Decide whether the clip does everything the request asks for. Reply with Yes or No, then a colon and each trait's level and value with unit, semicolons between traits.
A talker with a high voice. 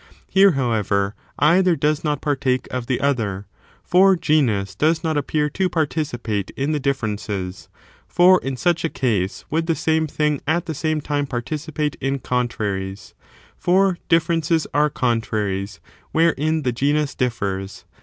No: medium, 145 Hz